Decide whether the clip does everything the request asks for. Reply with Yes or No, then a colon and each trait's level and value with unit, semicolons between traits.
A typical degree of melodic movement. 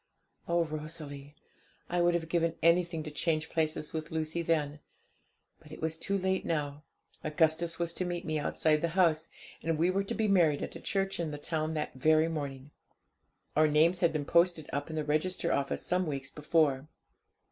No: narrow, 2.1 semitones